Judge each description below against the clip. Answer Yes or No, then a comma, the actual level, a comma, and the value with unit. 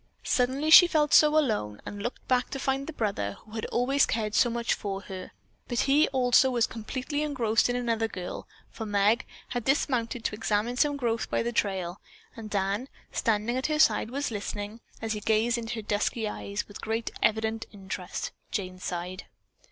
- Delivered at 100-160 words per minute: No, average, 185 wpm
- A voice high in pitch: Yes, high, 225 Hz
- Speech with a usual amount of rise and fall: Yes, average, 3.6 semitones